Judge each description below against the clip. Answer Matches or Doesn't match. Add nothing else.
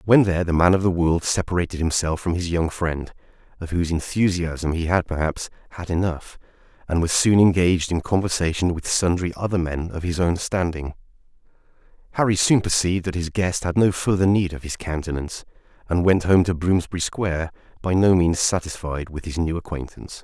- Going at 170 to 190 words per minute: Matches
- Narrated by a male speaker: Matches